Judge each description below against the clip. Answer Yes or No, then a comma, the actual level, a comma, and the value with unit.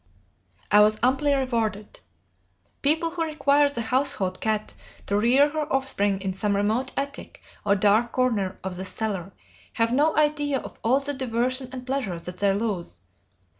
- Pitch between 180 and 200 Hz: No, high, 235 Hz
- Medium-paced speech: Yes, average, 160 wpm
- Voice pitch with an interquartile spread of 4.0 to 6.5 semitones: Yes, average, 5.3 semitones